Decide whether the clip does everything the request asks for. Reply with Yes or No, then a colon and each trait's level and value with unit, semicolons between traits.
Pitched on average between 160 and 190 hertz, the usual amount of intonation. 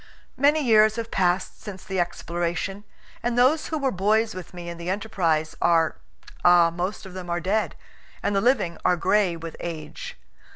Yes: medium, 185 Hz; average, 4.1 semitones